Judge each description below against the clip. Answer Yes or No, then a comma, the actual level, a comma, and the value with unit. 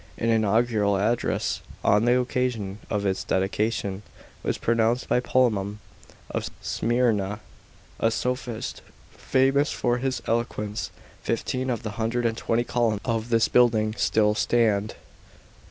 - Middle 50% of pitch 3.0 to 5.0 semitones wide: No, narrow, 2.5 semitones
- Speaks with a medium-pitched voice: No, low, 115 Hz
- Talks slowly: Yes, slow, 125 wpm